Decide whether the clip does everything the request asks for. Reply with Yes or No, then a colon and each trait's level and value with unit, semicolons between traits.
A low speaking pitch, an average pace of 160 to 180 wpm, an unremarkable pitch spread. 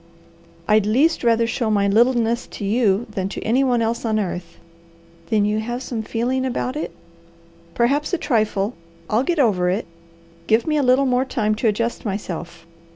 No: high, 230 Hz; average, 170 wpm; average, 3.2 semitones